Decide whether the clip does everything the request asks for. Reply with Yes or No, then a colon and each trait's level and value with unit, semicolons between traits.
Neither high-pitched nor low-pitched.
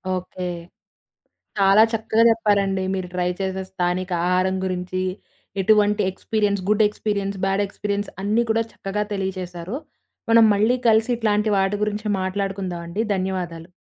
No: high, 195 Hz